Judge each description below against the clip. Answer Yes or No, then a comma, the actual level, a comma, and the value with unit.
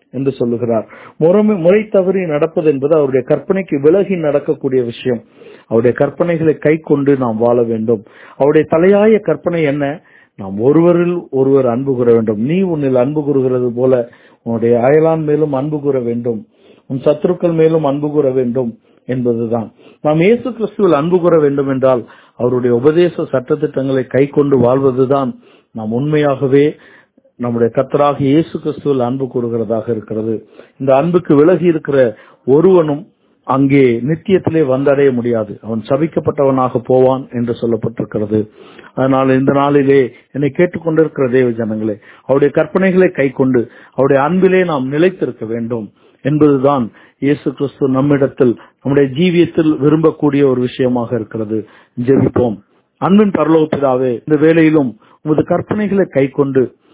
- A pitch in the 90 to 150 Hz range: Yes, medium, 140 Hz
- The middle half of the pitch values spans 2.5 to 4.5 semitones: Yes, average, 4.1 semitones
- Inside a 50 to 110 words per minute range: No, average, 120 wpm